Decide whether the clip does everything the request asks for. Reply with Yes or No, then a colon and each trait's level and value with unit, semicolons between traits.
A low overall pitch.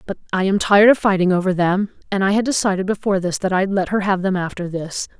No: high, 190 Hz